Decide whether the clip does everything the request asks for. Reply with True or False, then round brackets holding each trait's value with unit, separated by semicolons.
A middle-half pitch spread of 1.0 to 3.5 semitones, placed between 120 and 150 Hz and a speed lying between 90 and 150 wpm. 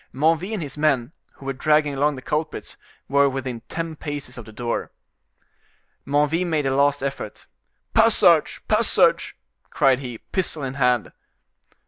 True (2.7 semitones; 140 Hz; 145 wpm)